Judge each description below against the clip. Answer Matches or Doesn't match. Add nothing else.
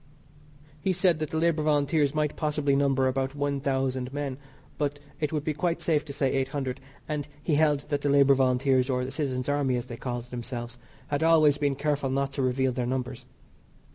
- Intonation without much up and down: Matches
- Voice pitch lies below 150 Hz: Matches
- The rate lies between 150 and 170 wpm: Doesn't match